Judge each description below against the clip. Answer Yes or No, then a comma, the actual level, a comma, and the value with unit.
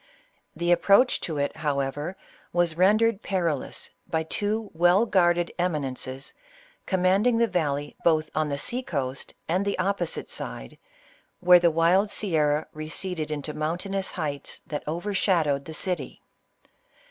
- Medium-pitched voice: Yes, medium, 170 Hz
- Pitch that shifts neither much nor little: Yes, average, 4.0 semitones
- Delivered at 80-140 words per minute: Yes, slow, 135 wpm